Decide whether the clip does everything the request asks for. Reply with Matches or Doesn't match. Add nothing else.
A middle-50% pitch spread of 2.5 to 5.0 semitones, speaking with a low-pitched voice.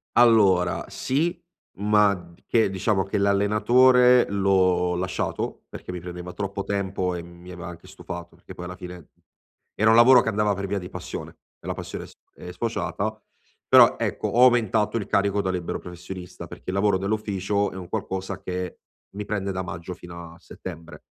Matches